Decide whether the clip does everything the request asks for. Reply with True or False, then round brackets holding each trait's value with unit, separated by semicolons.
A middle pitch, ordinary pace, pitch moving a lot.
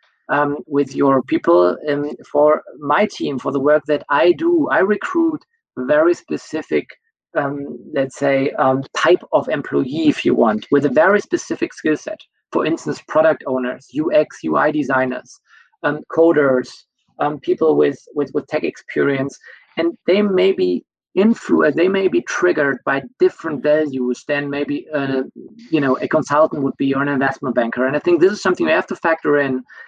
True (150 Hz; 170 wpm; 7.0 semitones)